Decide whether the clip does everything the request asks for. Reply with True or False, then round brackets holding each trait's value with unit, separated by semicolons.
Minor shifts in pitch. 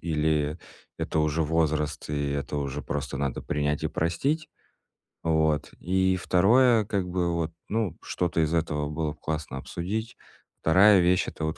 False (3.5 semitones)